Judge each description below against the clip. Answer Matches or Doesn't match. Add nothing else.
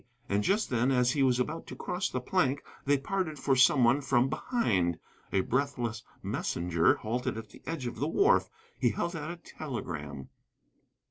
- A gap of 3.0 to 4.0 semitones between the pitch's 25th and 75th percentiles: Doesn't match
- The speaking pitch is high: Doesn't match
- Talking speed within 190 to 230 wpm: Doesn't match